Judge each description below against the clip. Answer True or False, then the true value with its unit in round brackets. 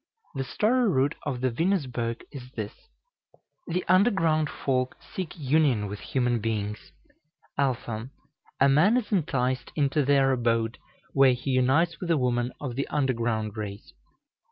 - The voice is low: True (130 Hz)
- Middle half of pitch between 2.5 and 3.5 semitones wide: False (4.4 semitones)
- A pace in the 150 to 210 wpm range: False (140 wpm)